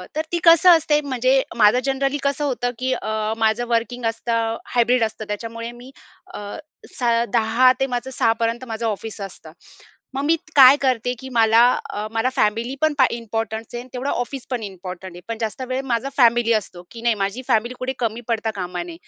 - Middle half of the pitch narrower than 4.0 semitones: Yes, narrow, 2.6 semitones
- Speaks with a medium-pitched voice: No, high, 235 Hz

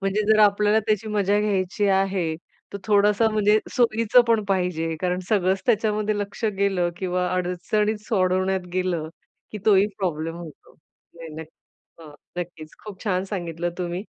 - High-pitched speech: Yes, high, 195 Hz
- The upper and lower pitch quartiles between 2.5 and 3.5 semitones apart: Yes, average, 2.8 semitones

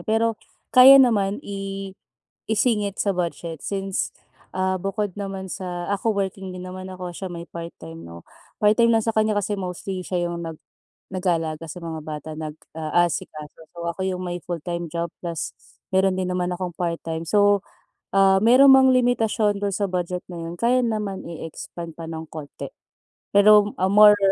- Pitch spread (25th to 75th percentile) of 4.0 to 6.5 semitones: No, average, 3.3 semitones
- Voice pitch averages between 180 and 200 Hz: Yes, medium, 185 Hz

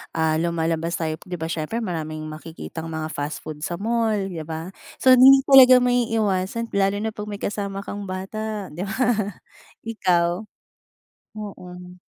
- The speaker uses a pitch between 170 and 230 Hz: Yes, high, 190 Hz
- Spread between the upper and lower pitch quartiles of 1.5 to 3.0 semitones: No, average, 5.0 semitones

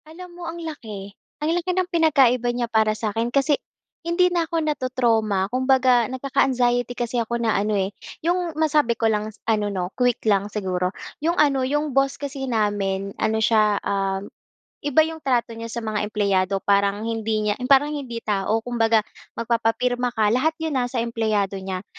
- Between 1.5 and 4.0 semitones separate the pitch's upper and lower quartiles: No, average, 4.6 semitones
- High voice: Yes, high, 235 Hz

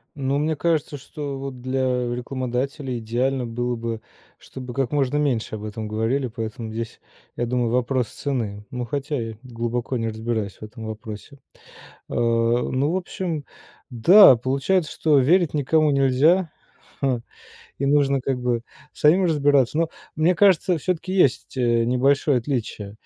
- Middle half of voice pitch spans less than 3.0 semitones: No, average, 3.7 semitones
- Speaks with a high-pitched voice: No, low, 130 Hz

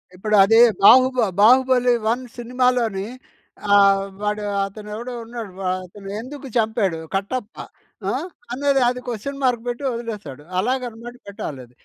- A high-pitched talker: Yes, high, 230 Hz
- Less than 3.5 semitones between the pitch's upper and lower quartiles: No, average, 3.8 semitones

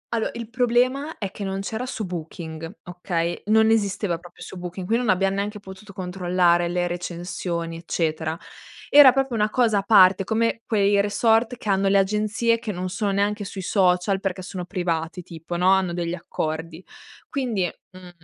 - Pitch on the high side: Yes, high, 195 Hz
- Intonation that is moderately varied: Yes, average, 3.4 semitones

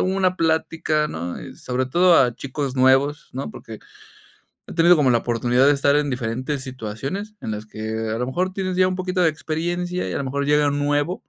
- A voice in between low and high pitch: Yes, medium, 145 Hz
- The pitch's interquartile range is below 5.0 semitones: No, average, 5.3 semitones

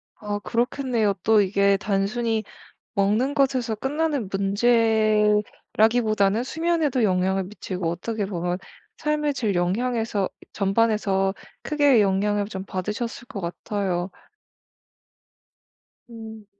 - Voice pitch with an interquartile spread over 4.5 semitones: No, average, 3.5 semitones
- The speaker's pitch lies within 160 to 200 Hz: No, high, 215 Hz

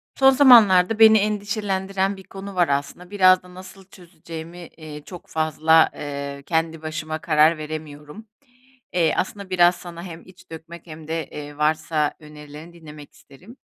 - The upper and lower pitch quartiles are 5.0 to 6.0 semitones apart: No, average, 3.5 semitones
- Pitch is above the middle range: No, medium, 165 Hz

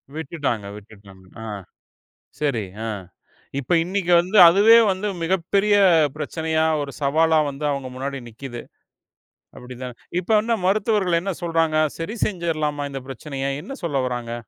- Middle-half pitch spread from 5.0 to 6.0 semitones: Yes, average, 5.3 semitones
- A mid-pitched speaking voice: Yes, medium, 155 Hz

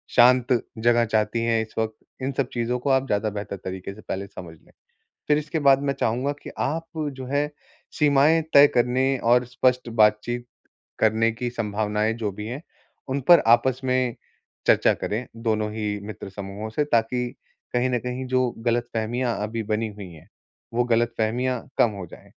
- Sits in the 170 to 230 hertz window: No, low, 120 Hz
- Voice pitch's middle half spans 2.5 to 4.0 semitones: Yes, average, 2.9 semitones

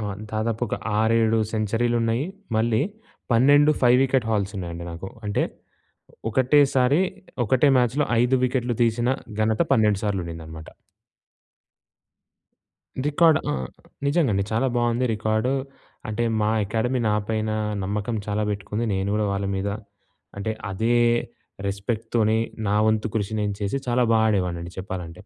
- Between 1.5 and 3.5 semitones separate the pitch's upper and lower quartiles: Yes, average, 3.2 semitones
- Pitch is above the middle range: No, low, 110 Hz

